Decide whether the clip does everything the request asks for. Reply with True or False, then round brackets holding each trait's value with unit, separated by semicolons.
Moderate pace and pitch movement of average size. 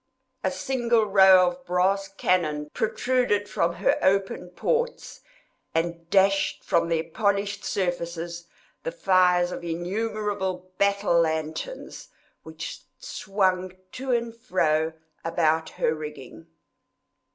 False (105 wpm; 3.4 semitones)